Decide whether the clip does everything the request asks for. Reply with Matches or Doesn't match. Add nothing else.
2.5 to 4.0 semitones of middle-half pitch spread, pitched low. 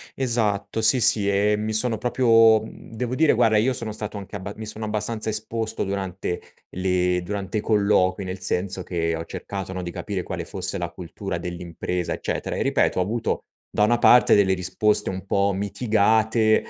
Matches